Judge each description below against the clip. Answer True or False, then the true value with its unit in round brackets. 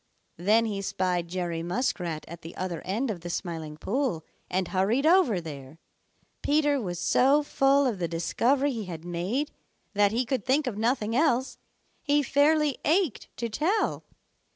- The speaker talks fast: False (160 wpm)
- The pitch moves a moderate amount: False (7.9 semitones)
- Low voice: False (220 Hz)